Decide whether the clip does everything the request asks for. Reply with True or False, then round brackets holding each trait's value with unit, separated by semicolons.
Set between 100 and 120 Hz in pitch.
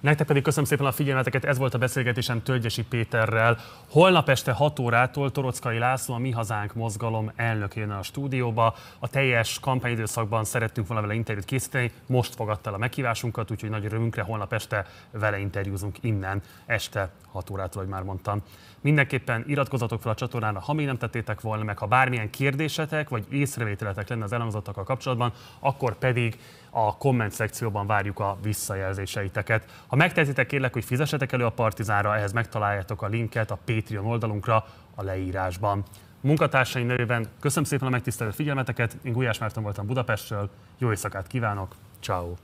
True (115 Hz)